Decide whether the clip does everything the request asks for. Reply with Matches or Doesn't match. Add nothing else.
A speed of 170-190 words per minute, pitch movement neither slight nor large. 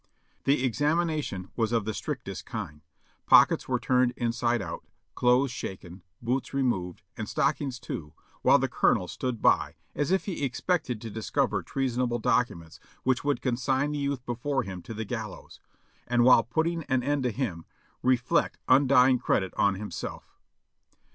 Doesn't match